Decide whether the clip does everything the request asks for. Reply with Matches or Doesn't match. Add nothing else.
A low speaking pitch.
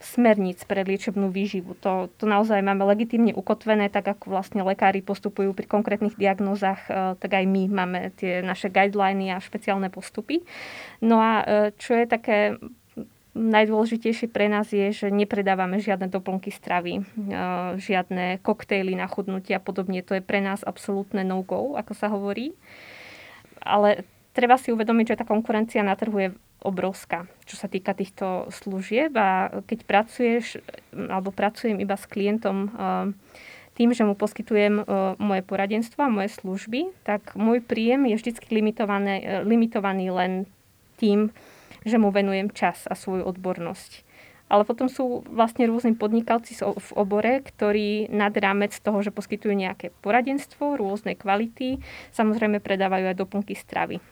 Doesn't match